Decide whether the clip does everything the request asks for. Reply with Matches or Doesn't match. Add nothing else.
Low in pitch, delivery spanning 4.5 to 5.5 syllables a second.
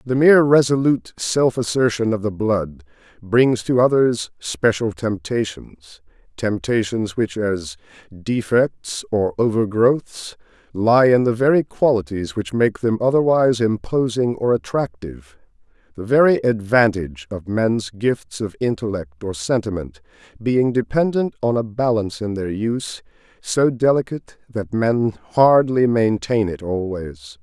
Doesn't match